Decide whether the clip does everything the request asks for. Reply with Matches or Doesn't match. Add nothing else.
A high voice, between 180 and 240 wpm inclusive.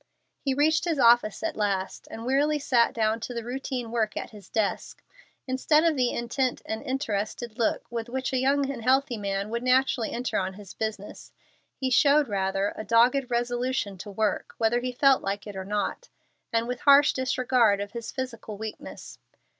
Matches